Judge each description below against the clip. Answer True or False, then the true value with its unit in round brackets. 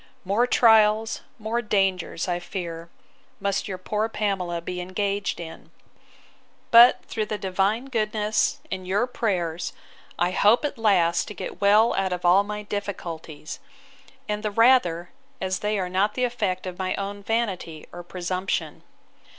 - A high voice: True (200 Hz)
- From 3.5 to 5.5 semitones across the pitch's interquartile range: False (2.9 semitones)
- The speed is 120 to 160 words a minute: True (150 wpm)